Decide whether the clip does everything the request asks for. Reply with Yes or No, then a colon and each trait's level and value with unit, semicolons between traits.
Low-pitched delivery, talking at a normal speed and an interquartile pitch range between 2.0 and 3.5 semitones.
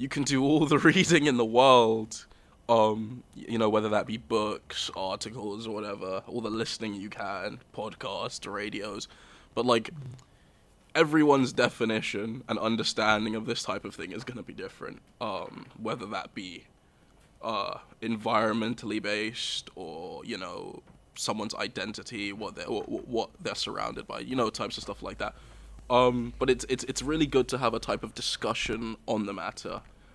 Yes: low, 115 Hz; average, 165 wpm; average, 3.0 semitones